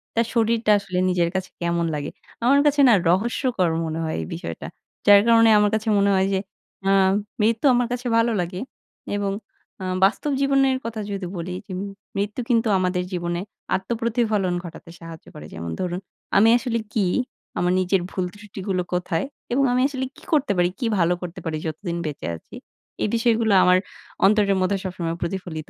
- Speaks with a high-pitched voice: Yes, high, 195 Hz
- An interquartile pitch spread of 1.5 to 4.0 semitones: No, average, 4.5 semitones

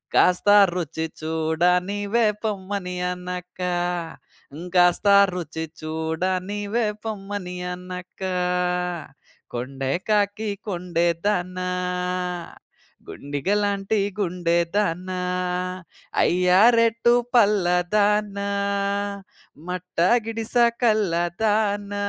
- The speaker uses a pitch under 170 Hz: No, medium, 185 Hz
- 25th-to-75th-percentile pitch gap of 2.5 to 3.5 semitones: Yes, average, 2.9 semitones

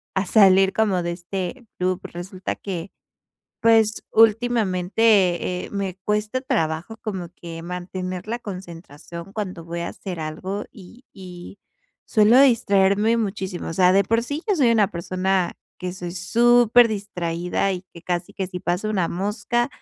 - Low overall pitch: No, high, 190 Hz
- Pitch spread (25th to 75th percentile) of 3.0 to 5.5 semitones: Yes, average, 3.5 semitones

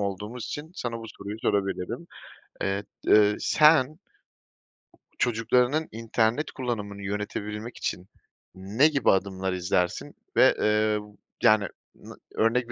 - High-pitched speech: No, low, 110 Hz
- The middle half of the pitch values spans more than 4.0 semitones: No, average, 3.5 semitones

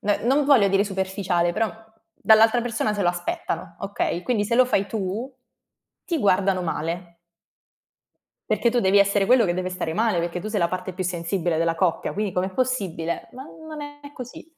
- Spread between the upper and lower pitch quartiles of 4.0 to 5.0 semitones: Yes, average, 4.7 semitones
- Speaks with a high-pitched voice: Yes, high, 195 Hz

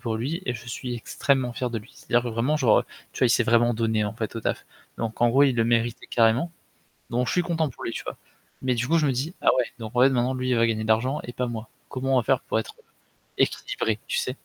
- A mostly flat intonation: Yes, narrow, 2.3 semitones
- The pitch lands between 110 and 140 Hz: Yes, low, 120 Hz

